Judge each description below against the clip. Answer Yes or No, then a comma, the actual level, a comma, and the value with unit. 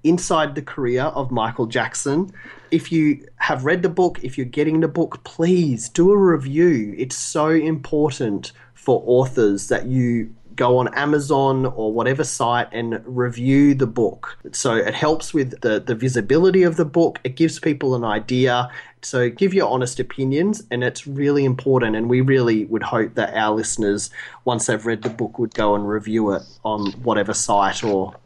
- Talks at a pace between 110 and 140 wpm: No, average, 180 wpm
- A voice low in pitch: Yes, low, 130 Hz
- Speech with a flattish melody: No, average, 4.9 semitones